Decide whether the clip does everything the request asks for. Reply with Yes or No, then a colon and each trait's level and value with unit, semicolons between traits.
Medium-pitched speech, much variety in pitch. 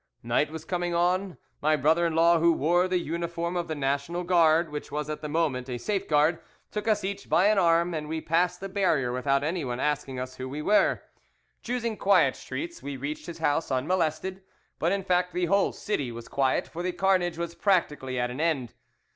No: medium, 165 Hz; average, 3.7 semitones